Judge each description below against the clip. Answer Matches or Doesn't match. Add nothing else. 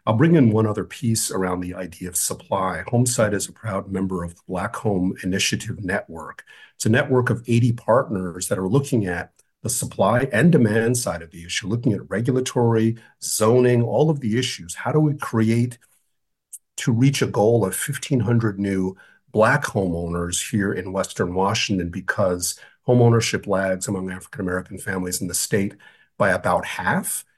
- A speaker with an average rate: Matches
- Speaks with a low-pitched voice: Matches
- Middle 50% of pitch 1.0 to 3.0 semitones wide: Doesn't match